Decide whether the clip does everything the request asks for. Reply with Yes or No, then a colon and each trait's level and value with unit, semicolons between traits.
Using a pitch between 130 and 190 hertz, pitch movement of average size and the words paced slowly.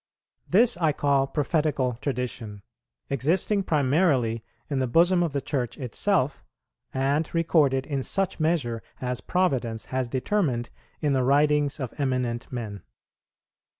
Yes: medium, 140 Hz; average, 4.2 semitones; slow, 125 wpm